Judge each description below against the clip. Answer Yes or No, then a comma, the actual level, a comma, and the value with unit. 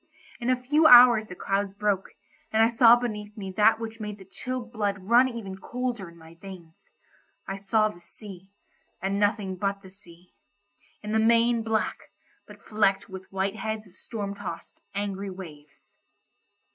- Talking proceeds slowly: No, average, 165 wpm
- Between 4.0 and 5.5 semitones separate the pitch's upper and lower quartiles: No, average, 2.9 semitones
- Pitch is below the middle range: No, high, 205 Hz